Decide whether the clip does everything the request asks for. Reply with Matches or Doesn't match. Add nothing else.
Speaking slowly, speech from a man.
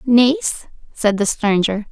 Doesn't match